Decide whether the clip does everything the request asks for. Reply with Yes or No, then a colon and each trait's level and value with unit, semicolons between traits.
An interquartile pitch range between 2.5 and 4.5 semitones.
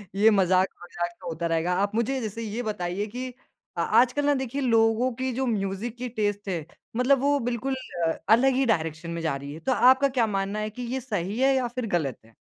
No: wide, 5.6 semitones